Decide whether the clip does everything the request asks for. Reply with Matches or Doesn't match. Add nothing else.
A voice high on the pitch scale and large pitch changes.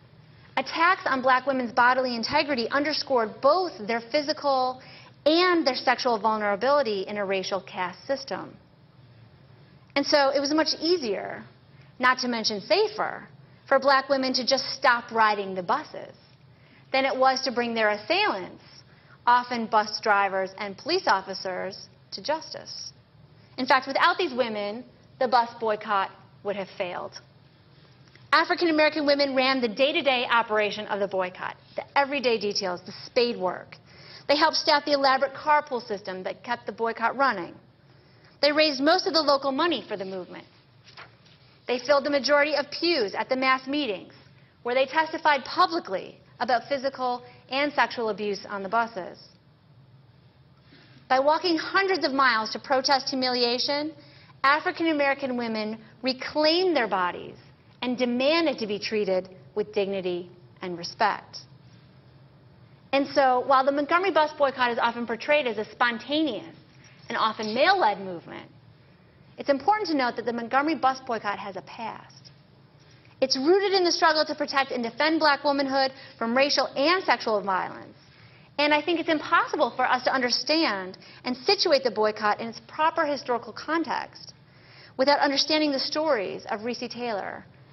Matches